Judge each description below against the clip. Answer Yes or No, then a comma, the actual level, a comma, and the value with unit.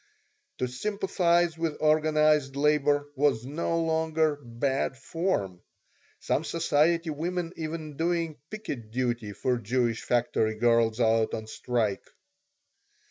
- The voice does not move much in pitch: No, average, 5.3 semitones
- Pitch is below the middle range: No, medium, 145 Hz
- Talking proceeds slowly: Yes, slow, 110 wpm